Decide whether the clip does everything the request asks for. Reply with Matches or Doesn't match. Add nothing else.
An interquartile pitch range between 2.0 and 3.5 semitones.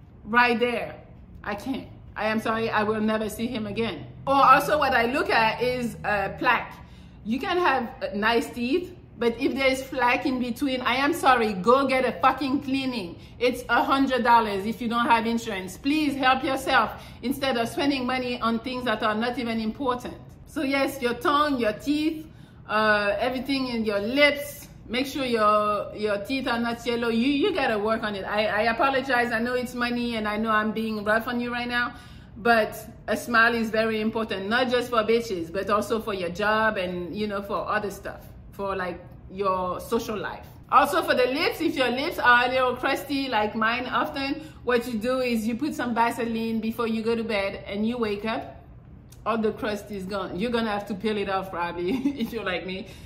Matches